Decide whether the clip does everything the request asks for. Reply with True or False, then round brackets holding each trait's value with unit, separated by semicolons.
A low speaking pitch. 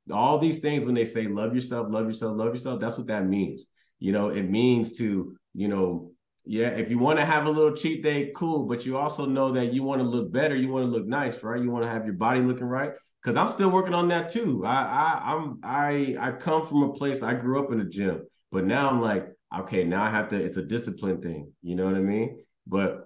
True (120 Hz)